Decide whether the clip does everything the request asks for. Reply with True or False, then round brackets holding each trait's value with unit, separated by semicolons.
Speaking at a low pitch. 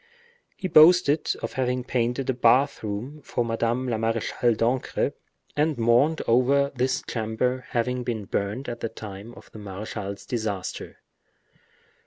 True (120 Hz)